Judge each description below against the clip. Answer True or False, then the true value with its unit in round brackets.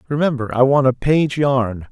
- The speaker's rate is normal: True (190 wpm)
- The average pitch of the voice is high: False (135 Hz)